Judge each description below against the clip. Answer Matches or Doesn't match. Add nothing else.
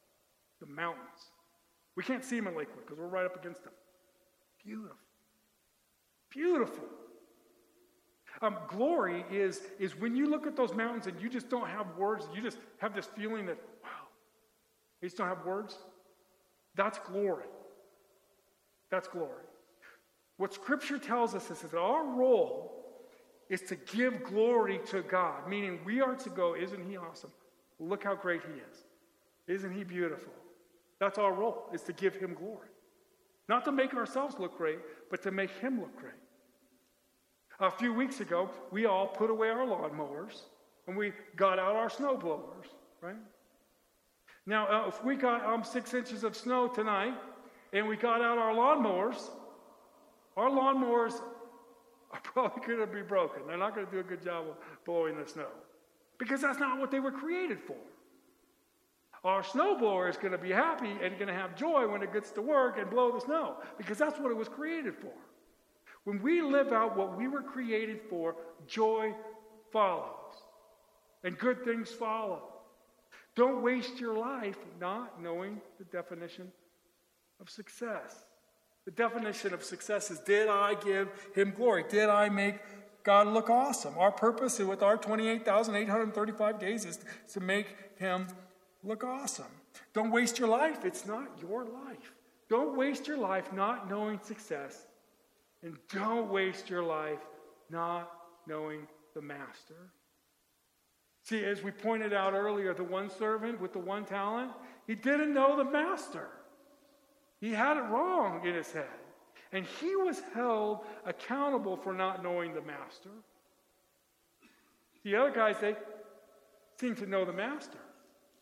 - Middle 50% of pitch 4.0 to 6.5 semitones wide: Matches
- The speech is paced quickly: Doesn't match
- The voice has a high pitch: Matches